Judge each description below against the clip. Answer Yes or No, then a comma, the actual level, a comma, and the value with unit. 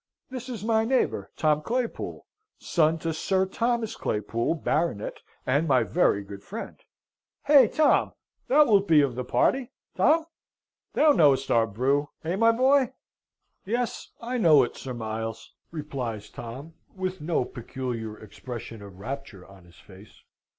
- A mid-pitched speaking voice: Yes, medium, 150 Hz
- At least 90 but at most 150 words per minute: Yes, average, 145 wpm